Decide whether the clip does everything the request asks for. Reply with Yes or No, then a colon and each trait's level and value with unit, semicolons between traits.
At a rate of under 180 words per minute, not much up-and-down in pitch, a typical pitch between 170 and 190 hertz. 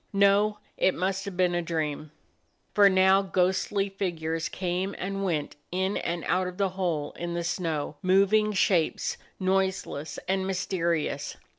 Yes: average, 150 wpm; narrow, 2.3 semitones; medium, 185 Hz